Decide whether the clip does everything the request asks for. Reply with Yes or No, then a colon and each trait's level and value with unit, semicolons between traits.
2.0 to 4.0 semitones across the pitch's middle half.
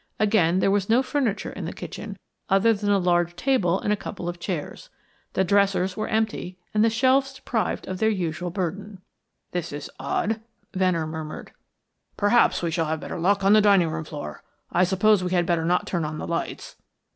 Yes: average, 3.6 semitones